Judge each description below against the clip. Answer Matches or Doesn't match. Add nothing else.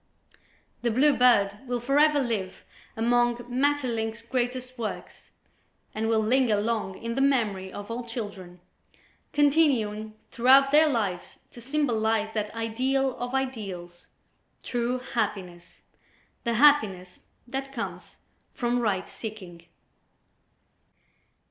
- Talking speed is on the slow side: Matches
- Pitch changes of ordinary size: Matches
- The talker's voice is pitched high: Matches